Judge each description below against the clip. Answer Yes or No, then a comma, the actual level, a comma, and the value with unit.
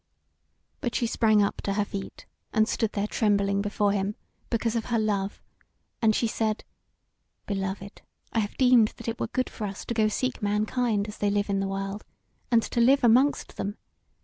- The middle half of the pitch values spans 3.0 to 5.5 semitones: No, narrow, 2.4 semitones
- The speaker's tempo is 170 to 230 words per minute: Yes, average, 190 wpm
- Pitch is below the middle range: No, high, 215 Hz